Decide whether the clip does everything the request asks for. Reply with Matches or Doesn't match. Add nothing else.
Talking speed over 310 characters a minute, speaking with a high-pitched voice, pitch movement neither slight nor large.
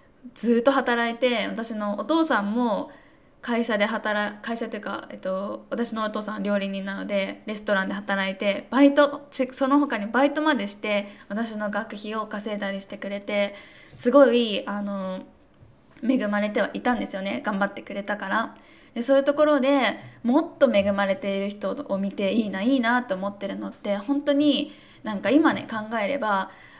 Matches